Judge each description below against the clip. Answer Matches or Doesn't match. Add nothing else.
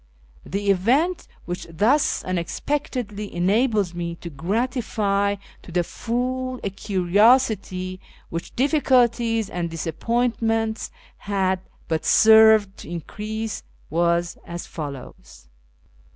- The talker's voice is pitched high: Matches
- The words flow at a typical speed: Doesn't match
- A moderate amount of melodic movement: Matches